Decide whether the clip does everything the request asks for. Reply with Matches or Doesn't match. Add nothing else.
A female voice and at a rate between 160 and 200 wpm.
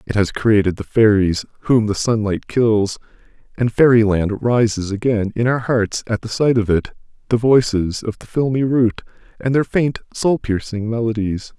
Doesn't match